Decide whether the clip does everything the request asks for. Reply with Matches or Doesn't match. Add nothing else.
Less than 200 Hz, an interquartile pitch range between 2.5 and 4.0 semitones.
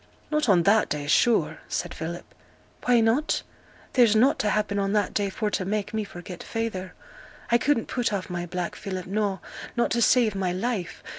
Doesn't match